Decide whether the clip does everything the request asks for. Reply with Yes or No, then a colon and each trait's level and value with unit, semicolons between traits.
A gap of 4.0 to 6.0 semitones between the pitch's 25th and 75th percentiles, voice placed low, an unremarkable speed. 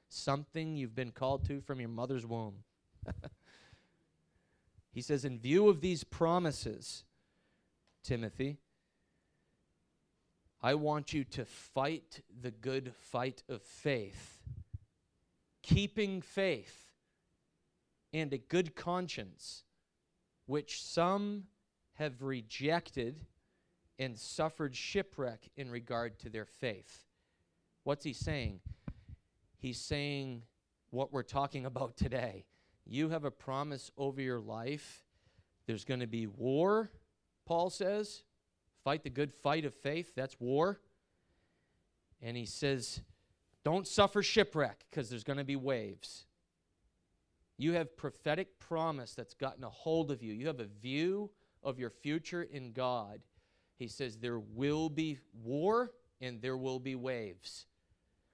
No: average, 4.9 semitones; low, 130 Hz; slow, 120 wpm